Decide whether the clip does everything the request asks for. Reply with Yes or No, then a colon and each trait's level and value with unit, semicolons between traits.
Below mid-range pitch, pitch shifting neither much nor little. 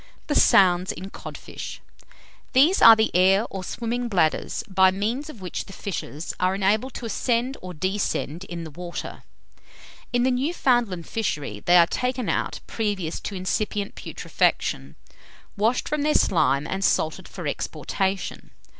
No: high, 195 Hz; average, 4.7 semitones